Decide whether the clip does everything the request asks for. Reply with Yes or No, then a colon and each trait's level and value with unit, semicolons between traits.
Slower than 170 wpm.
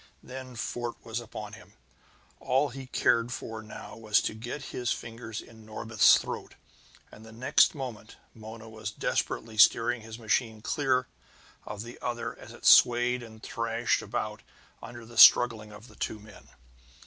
Yes: average, 160 wpm